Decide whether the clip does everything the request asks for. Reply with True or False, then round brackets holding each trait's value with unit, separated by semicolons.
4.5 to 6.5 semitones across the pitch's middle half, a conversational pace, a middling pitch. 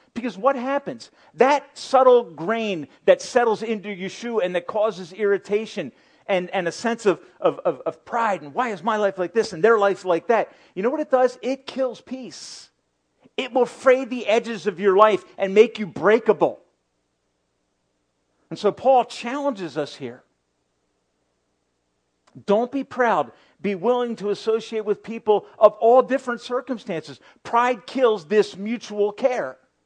False (4.8 semitones; 160 wpm; 215 Hz)